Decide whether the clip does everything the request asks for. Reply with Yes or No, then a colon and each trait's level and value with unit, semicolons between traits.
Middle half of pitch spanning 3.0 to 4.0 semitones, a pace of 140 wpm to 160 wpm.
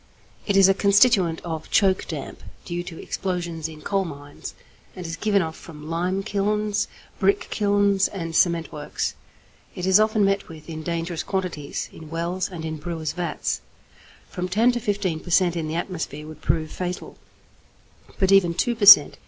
No: average, 3.4 semitones; average, 175 wpm